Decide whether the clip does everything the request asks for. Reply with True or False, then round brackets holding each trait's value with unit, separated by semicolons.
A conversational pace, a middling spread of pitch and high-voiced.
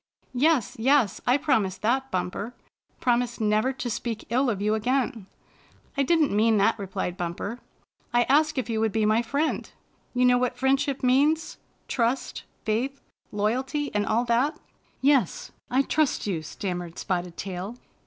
True (160 wpm; 4.1 semitones; 240 Hz)